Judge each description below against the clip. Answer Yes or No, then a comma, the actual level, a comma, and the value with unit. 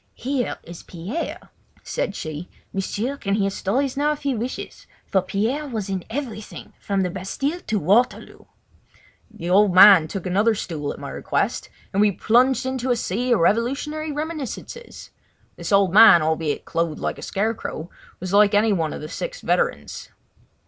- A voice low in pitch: No, high, 210 Hz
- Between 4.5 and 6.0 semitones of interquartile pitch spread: Yes, wide, 5.6 semitones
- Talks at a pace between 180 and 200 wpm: No, average, 165 wpm